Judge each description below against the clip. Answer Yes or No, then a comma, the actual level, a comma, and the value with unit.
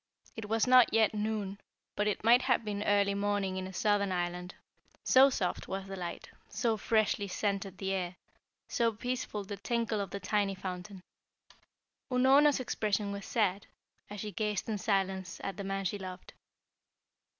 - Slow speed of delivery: No, average, 165 wpm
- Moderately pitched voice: No, high, 205 Hz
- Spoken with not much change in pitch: Yes, narrow, 2.3 semitones